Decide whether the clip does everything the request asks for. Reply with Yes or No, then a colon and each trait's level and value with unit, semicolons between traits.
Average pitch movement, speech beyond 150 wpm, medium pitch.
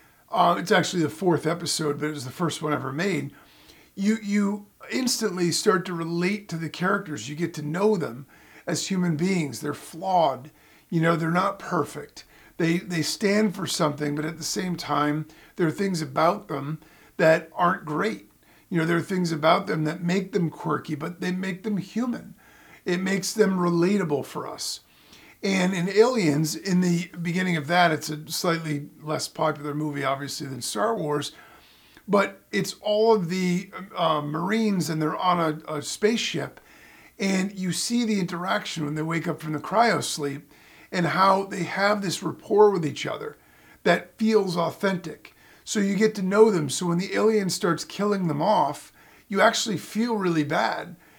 Yes: average, 4.2 semitones; average, 180 wpm; medium, 175 Hz